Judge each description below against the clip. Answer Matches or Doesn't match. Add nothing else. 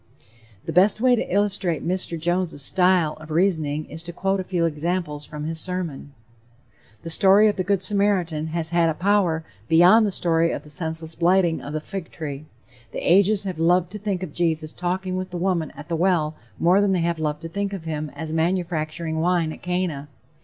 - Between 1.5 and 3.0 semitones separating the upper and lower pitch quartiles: Matches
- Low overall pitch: Doesn't match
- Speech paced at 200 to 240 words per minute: Matches